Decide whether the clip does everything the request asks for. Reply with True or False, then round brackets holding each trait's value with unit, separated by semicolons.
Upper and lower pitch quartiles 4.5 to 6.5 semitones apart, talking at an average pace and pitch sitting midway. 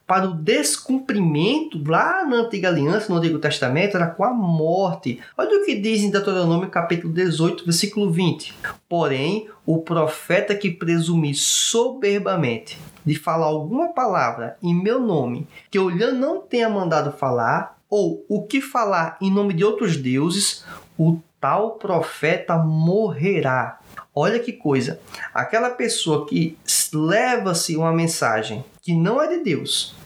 True (4.8 semitones; 140 wpm; 180 Hz)